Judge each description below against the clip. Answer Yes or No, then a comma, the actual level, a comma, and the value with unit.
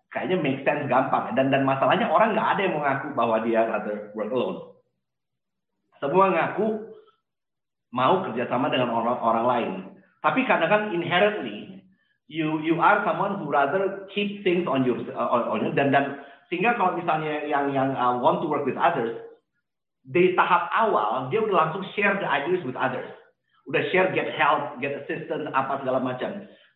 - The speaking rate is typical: No, fast, 170 wpm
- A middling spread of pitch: No, wide, 6.7 semitones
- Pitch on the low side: No, medium, 160 Hz